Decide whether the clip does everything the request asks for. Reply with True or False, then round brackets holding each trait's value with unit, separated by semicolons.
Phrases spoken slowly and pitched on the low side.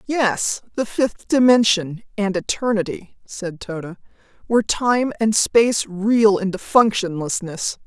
False (115 wpm; 205 Hz)